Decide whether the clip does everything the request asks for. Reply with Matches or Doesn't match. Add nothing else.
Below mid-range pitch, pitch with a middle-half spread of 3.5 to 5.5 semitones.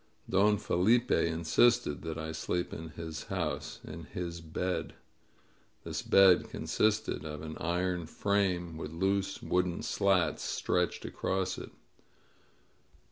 Doesn't match